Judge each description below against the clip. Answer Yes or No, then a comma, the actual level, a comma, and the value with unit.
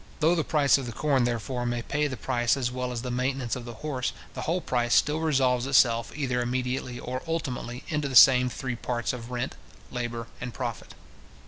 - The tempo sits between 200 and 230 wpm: Yes, fast, 205 wpm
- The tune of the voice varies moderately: No, narrow, 2.2 semitones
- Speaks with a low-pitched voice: Yes, low, 125 Hz